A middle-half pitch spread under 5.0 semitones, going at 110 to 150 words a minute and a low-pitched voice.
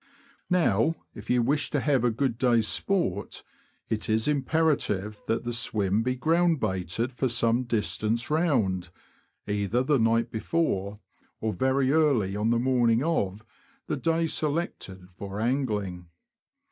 No: average, 5.3 semitones; average, 140 wpm; low, 120 Hz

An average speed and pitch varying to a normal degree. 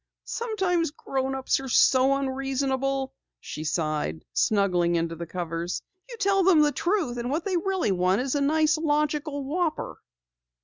No: average, 145 wpm; wide, 8.1 semitones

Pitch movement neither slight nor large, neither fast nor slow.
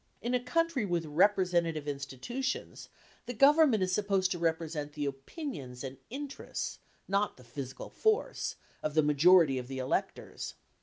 No: wide, 9.0 semitones; average, 145 wpm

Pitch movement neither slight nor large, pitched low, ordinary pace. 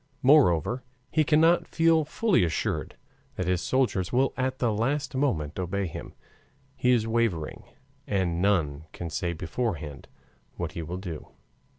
No: wide, 7.5 semitones; low, 100 Hz; average, 145 wpm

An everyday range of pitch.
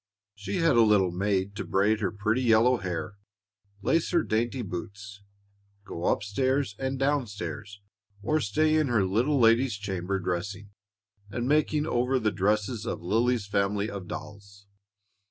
Yes: average, 3.9 semitones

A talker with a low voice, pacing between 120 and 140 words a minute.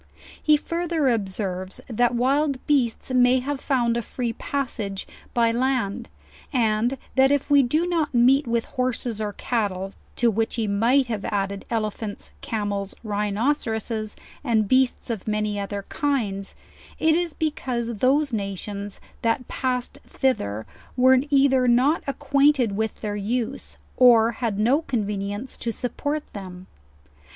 No: high, 235 Hz; slow, 135 wpm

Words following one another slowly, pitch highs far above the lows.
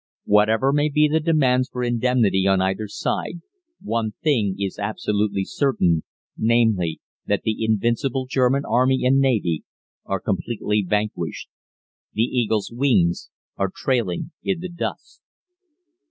No: slow, 125 wpm; average, 4.5 semitones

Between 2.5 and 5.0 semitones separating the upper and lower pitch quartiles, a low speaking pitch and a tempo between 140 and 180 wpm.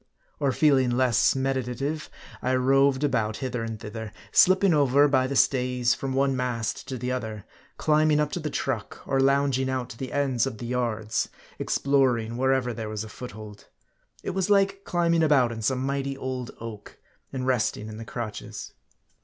Yes: average, 2.9 semitones; low, 130 Hz; average, 175 wpm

